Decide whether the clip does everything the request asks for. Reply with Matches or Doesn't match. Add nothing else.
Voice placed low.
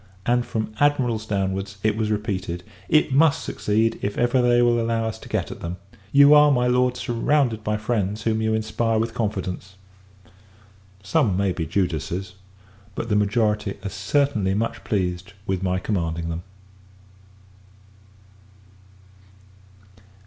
Matches